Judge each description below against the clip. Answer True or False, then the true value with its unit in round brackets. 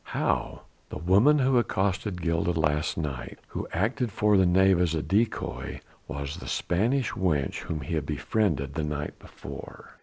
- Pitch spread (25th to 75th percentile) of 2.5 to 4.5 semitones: False (5.5 semitones)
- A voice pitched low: True (90 Hz)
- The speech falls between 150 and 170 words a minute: True (160 wpm)